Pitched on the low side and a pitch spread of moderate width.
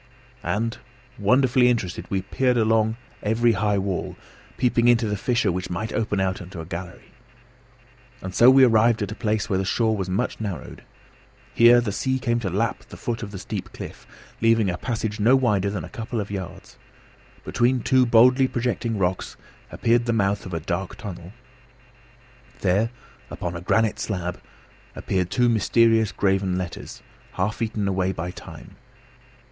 Yes: low, 110 Hz; average, 3.7 semitones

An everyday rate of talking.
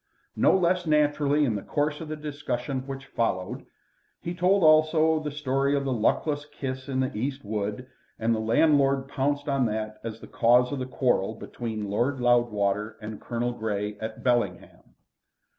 Yes: average, 170 wpm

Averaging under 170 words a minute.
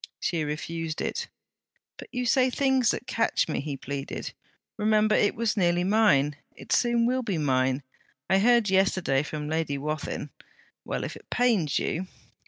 Yes: average, 160 wpm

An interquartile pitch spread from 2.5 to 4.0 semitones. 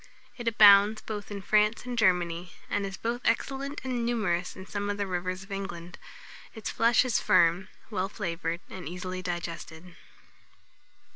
Yes: average, 3.7 semitones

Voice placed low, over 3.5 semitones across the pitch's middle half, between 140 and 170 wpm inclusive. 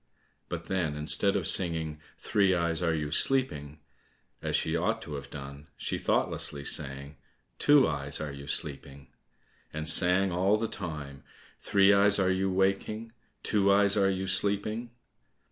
Yes: very low, 90 Hz; average, 5.1 semitones; average, 150 wpm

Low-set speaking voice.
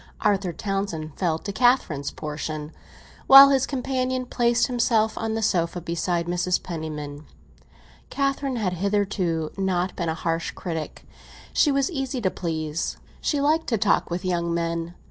No: medium, 185 Hz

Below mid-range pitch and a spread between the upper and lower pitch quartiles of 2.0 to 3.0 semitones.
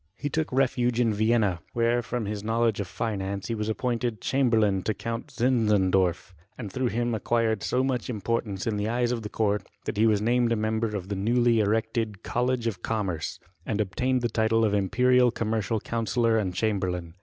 Yes: low, 110 Hz; average, 2.7 semitones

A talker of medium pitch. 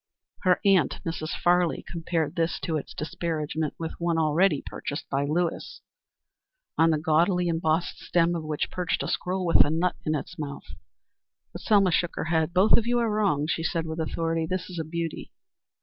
Yes: medium, 165 Hz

